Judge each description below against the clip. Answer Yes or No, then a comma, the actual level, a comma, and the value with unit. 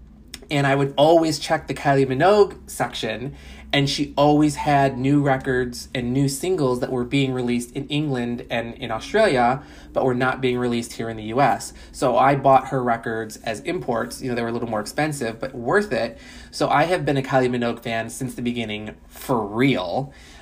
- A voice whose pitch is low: Yes, low, 130 Hz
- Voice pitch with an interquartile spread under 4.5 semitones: Yes, average, 3.1 semitones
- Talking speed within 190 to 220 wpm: Yes, average, 195 wpm